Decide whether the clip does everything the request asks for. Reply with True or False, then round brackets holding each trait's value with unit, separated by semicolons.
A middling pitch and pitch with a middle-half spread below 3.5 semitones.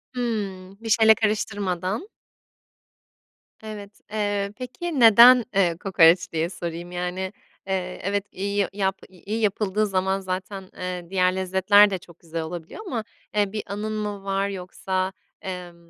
False (195 Hz; 2.4 semitones)